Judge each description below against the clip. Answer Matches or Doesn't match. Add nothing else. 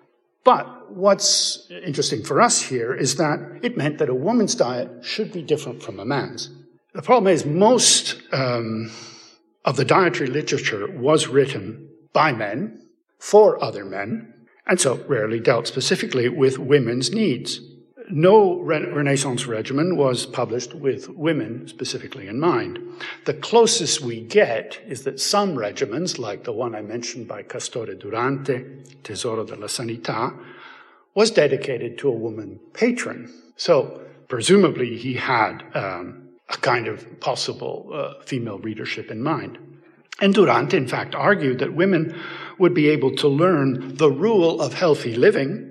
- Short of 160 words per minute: Matches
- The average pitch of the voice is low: Doesn't match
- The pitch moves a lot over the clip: Matches